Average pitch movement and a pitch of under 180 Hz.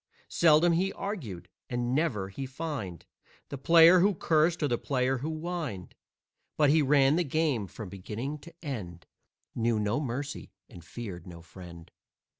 No: wide, 7.4 semitones; low, 135 Hz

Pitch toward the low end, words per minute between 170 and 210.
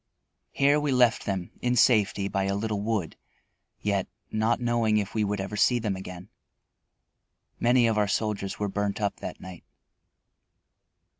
No: low, 105 Hz; average, 155 wpm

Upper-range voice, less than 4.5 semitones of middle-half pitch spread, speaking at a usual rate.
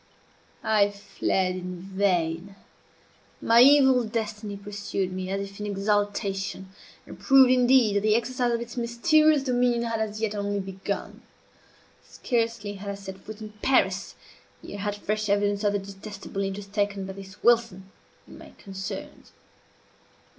Yes: high, 205 Hz; average, 2.8 semitones; average, 150 wpm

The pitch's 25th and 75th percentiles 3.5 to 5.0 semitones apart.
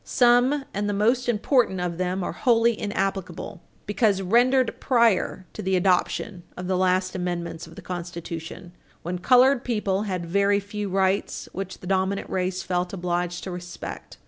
No: average, 2.9 semitones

